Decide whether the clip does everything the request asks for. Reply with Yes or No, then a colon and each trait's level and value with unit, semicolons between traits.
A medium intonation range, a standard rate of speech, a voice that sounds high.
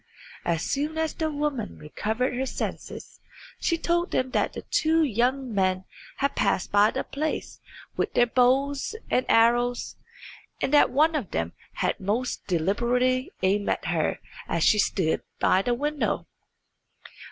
No: wide, 5.8 semitones; average, 145 wpm; very high, 250 Hz